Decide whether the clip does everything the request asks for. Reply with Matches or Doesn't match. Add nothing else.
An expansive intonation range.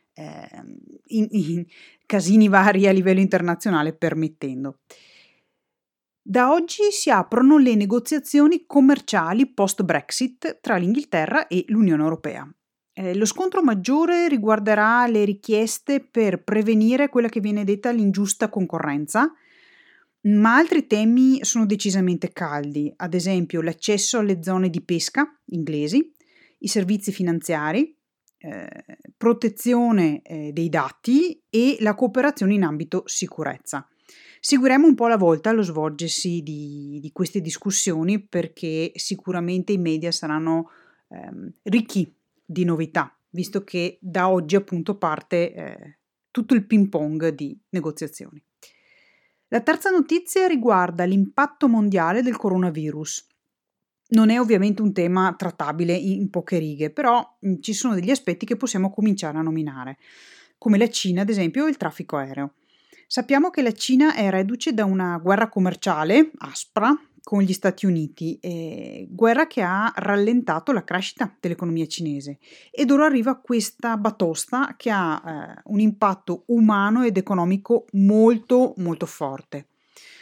Matches